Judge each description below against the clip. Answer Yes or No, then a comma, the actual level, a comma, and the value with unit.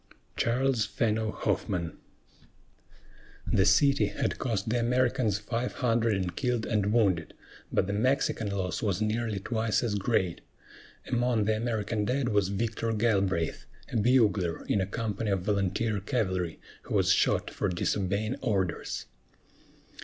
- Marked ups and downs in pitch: No, average, 3.2 semitones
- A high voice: No, low, 110 Hz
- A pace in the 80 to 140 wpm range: Yes, slow, 135 wpm